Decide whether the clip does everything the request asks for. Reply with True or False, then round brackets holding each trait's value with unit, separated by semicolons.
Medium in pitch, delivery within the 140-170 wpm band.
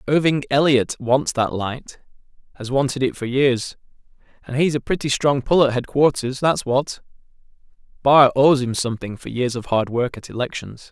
False (130 Hz; 160 wpm)